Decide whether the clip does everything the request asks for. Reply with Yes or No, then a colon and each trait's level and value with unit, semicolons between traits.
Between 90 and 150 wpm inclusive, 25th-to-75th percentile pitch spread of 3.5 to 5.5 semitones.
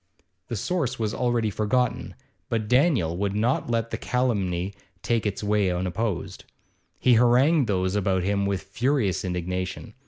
Yes: average, 145 wpm; average, 4.5 semitones